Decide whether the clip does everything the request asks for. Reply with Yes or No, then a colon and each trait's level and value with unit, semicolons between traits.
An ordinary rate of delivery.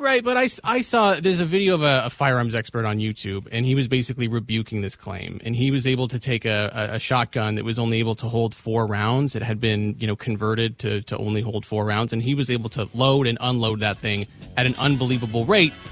No: fast, 245 wpm